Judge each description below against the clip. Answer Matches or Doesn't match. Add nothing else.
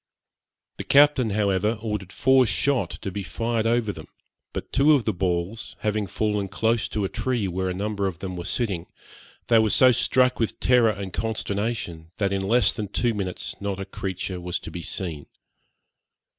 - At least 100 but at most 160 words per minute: Doesn't match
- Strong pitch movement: Doesn't match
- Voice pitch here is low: Matches